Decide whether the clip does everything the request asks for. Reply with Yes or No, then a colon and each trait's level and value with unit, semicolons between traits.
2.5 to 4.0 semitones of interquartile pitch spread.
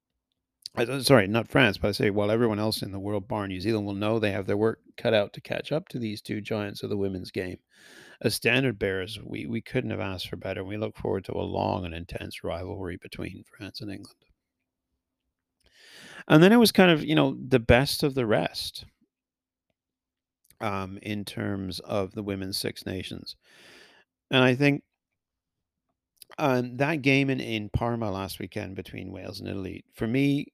No: average, 4.7 semitones